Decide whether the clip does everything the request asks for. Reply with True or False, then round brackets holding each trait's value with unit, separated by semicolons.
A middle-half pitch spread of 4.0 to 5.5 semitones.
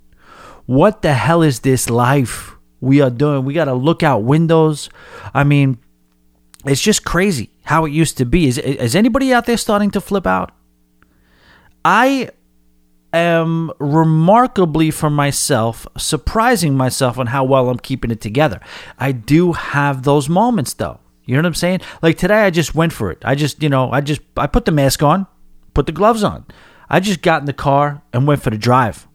True (5.0 semitones)